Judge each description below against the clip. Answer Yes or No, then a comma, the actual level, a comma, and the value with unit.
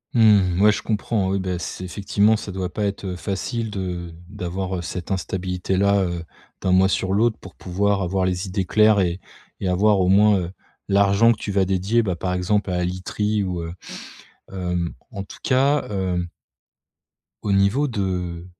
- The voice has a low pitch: Yes, very low, 95 Hz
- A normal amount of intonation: No, narrow, 2.2 semitones